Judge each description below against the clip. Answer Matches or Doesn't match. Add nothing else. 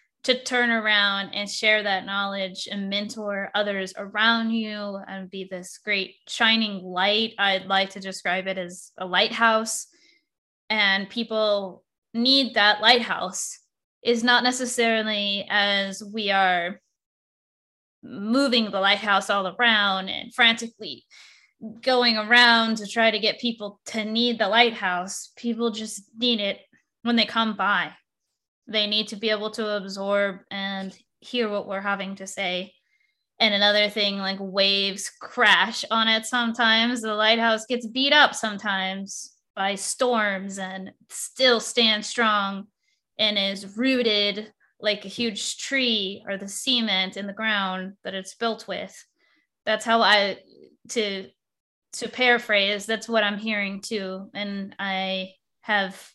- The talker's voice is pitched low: Doesn't match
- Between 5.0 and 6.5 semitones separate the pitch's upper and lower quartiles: Doesn't match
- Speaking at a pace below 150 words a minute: Matches